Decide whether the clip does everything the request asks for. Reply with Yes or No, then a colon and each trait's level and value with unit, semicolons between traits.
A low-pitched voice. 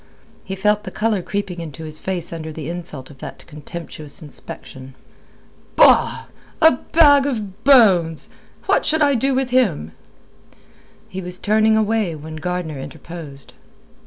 No: medium, 180 Hz